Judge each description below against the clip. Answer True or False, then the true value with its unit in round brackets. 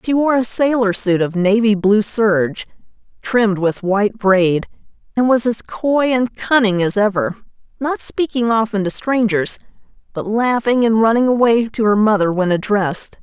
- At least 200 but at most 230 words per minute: False (165 wpm)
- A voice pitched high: True (215 Hz)